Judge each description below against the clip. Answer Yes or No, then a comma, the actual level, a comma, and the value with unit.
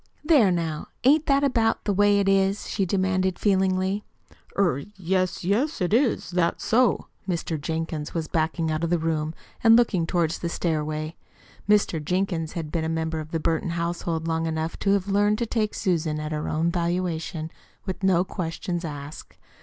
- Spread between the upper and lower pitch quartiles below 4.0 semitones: Yes, average, 3.5 semitones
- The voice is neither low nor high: Yes, medium, 175 Hz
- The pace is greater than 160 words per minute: Yes, average, 175 wpm